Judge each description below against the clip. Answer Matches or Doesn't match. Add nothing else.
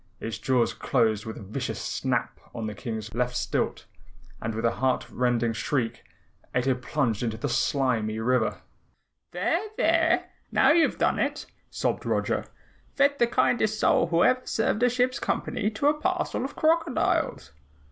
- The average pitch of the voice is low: Matches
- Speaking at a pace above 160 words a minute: Doesn't match